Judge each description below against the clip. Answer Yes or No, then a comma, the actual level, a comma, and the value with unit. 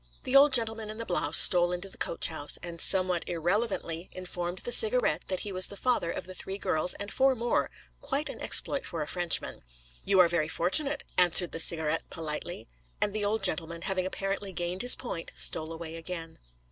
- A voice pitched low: No, medium, 185 Hz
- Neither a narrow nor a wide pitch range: Yes, average, 3.9 semitones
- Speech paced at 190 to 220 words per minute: Yes, average, 195 wpm